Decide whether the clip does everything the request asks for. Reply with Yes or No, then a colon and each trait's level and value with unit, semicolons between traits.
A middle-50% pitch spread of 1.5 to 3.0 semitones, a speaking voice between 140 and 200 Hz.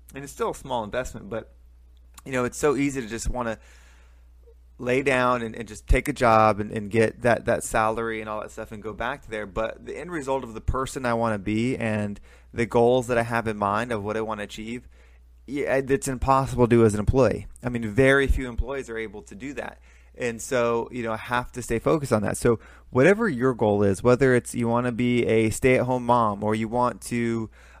No: average, 2.7 semitones; low, 115 Hz